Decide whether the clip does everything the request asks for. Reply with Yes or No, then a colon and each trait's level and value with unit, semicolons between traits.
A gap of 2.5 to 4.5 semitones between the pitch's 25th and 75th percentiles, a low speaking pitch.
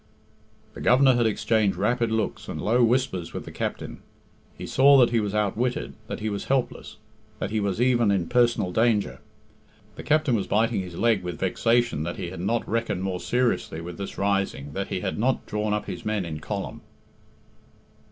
Yes: average, 3.7 semitones; low, 105 Hz